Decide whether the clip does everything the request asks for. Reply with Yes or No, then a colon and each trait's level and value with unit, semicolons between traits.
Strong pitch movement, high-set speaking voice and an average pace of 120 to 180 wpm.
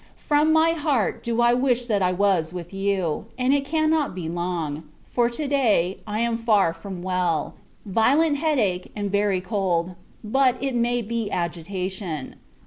Yes: wide, 5.7 semitones; high, 210 Hz; average, 165 wpm